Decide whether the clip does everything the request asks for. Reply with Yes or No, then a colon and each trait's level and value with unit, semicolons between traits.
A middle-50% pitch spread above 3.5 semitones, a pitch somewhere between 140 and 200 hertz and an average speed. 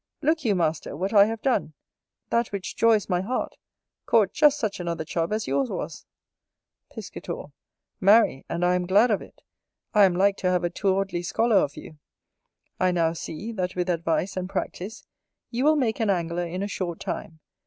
Yes: average, 4.0 semitones; high, 190 Hz; average, 185 wpm